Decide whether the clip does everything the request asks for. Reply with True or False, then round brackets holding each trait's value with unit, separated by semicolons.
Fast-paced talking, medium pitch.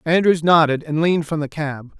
True (210 wpm; 160 Hz)